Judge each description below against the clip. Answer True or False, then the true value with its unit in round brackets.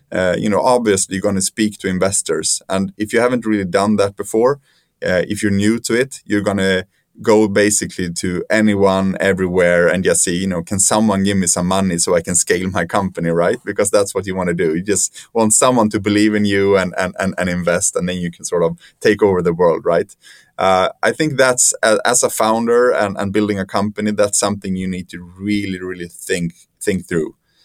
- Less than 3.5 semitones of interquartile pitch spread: True (2.4 semitones)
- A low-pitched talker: True (100 Hz)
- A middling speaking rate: False (220 wpm)